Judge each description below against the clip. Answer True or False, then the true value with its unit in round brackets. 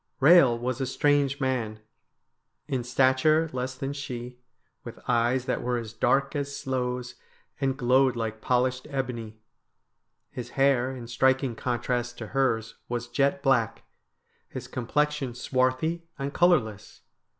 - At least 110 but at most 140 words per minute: True (135 wpm)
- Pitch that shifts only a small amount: True (2.2 semitones)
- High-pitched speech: False (130 Hz)